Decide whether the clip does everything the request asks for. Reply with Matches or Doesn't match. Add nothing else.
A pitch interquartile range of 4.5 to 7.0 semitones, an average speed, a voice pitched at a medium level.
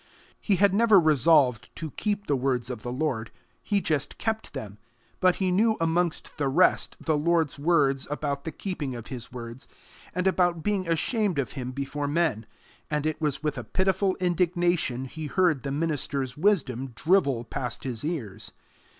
Matches